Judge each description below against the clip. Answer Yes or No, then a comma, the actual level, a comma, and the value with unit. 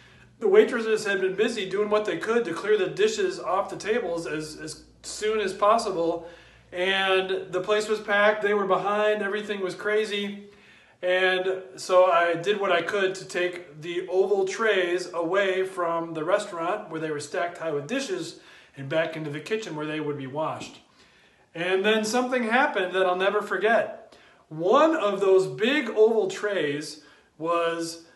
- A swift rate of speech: No, average, 170 wpm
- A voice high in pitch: Yes, high, 195 Hz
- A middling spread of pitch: Yes, average, 4.0 semitones